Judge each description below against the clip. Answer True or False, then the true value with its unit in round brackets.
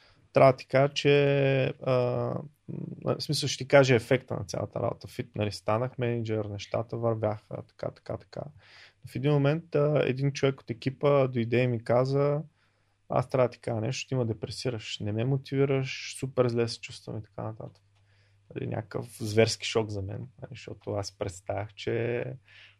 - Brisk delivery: True (170 wpm)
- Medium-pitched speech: False (120 Hz)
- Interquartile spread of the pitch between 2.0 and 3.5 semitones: False (4.0 semitones)